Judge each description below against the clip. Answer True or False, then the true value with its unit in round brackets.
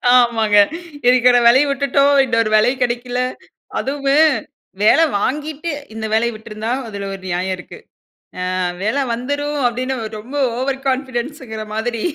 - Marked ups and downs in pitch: False (3.7 semitones)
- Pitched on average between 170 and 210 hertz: False (245 Hz)